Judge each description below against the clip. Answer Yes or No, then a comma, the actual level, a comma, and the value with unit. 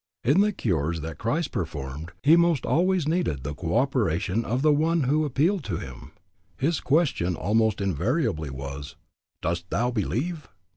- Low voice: Yes, low, 115 Hz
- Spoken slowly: No, average, 155 wpm